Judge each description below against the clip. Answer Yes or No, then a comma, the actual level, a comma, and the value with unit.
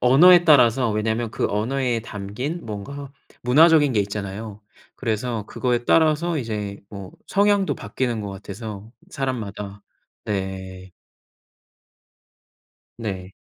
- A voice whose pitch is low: Yes, low, 115 Hz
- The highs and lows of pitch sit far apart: No, average, 5.0 semitones